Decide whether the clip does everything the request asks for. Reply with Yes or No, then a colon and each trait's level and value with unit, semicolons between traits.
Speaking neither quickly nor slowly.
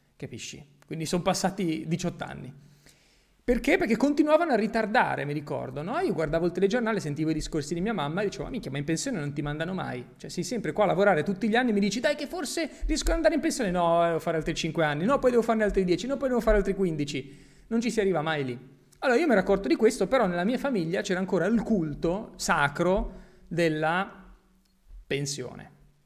No: fast, 225 wpm